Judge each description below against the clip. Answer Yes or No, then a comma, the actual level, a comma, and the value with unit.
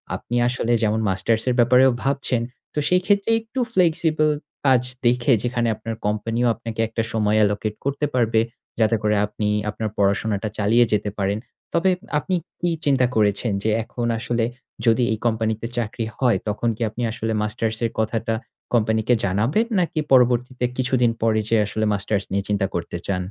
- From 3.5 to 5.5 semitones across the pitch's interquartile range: No, average, 2.9 semitones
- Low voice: Yes, low, 115 Hz